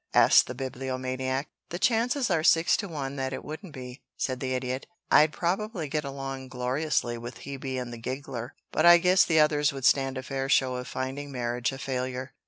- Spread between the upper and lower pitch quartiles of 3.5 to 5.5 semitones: No, average, 3.0 semitones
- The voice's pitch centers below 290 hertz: Yes, low, 135 Hz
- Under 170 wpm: No, average, 195 wpm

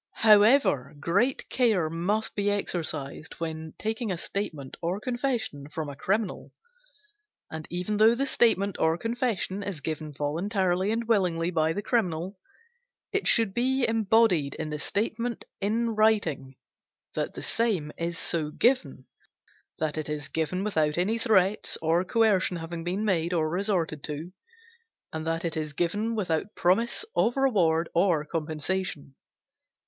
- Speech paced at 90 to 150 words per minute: Yes, average, 145 wpm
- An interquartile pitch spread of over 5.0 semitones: Yes, wide, 5.4 semitones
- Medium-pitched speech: Yes, medium, 180 Hz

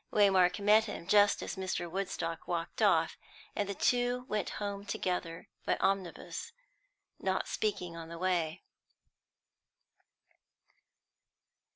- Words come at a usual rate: No, slow, 110 wpm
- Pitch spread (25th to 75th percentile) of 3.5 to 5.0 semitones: No, average, 2.9 semitones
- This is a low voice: No, high, 190 Hz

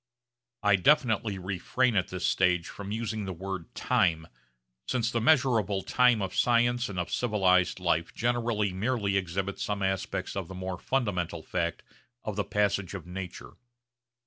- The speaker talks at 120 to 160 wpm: Yes, average, 150 wpm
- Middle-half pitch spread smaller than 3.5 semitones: No, average, 3.9 semitones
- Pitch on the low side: Yes, low, 100 Hz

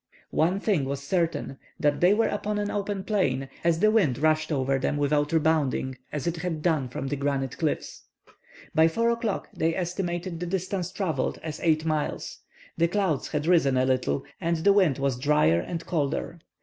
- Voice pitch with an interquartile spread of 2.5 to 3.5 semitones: No, average, 4.2 semitones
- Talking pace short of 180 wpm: No, average, 185 wpm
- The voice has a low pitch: No, medium, 160 Hz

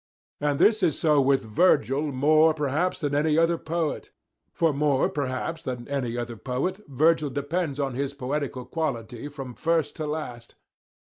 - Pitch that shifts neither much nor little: Yes, average, 3.2 semitones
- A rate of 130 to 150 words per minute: No, average, 160 wpm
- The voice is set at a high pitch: No, medium, 145 Hz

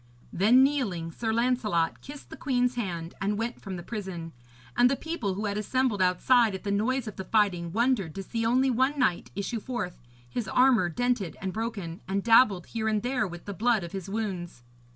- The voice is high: Yes, high, 215 Hz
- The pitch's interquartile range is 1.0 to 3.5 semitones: No, average, 4.8 semitones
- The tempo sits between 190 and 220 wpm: Yes, average, 200 wpm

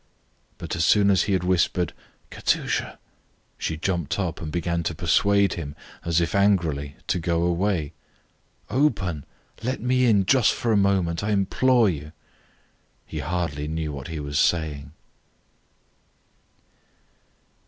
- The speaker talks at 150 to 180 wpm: No, slow, 135 wpm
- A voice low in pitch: Yes, very low, 85 Hz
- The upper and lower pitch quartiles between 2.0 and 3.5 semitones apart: No, average, 4.0 semitones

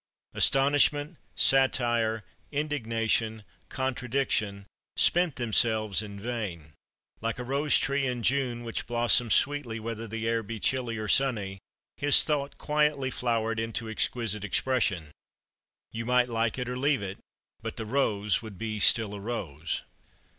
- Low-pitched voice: Yes, low, 115 Hz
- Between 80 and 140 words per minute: Yes, slow, 135 wpm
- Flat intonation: No, average, 3.3 semitones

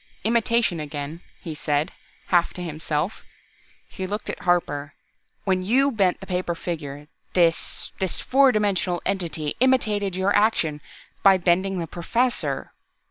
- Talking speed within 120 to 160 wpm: Yes, slow, 135 wpm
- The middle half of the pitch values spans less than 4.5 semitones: Yes, average, 4.1 semitones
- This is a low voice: No, medium, 180 Hz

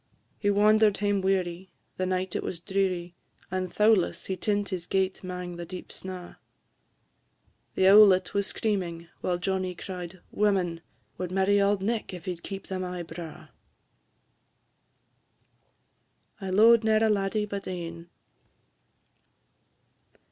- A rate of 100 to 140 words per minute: Yes, slow, 135 wpm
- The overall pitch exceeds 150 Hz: Yes, high, 190 Hz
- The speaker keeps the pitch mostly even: Yes, narrow, 2.1 semitones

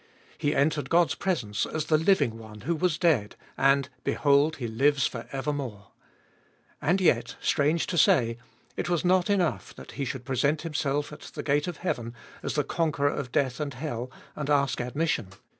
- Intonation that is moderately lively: Yes, average, 4.0 semitones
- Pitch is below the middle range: No, medium, 145 Hz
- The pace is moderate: Yes, average, 180 wpm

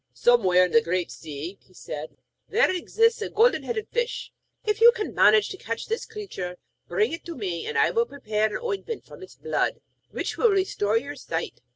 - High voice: Yes, very high, 330 Hz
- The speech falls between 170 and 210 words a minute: Yes, average, 200 wpm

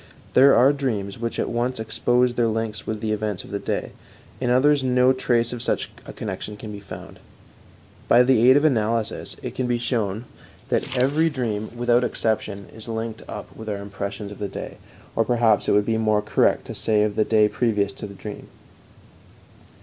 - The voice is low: Yes, low, 115 Hz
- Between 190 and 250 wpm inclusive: Yes, average, 200 wpm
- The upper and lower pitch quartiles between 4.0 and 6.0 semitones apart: No, average, 2.8 semitones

